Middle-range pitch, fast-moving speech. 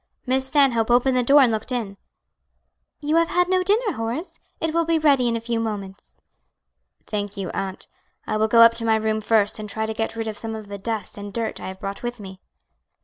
No: high, 225 Hz; fast, 230 wpm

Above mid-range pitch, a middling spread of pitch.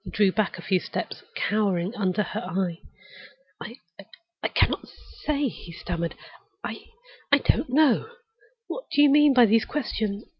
No: high, 215 Hz; wide, 6.9 semitones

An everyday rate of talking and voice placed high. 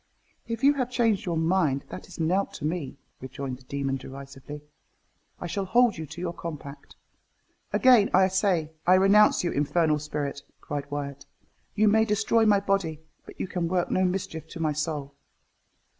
No: average, 175 wpm; medium, 170 Hz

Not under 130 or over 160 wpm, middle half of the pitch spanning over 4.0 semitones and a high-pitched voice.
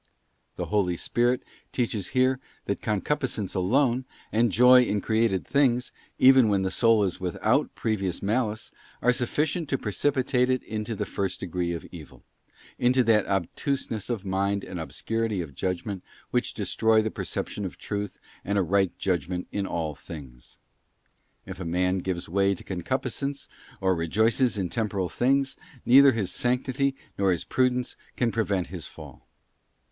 No: average, 155 wpm; average, 5.0 semitones; low, 105 Hz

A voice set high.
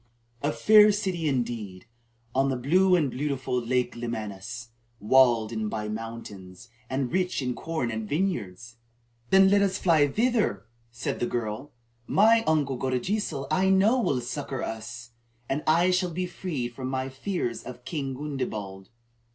No: low, 130 Hz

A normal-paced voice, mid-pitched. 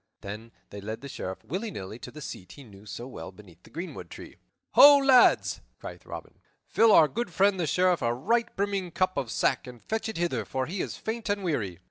No: fast, 220 wpm; medium, 160 Hz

